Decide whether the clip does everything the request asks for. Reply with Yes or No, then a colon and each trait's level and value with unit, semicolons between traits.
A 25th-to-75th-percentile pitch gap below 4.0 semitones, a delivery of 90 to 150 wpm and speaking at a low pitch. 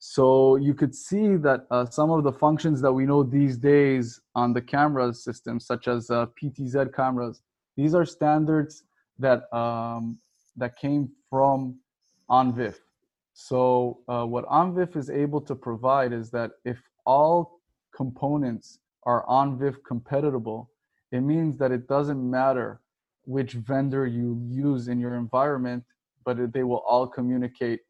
Yes: narrow, 2.6 semitones; average, 145 wpm; low, 130 Hz